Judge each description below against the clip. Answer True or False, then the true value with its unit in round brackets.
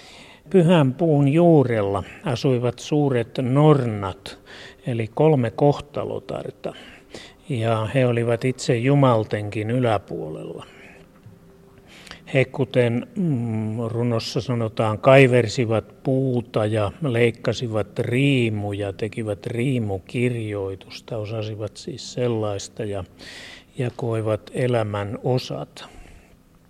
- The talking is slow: True (75 wpm)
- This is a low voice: True (120 Hz)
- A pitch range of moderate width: True (3.4 semitones)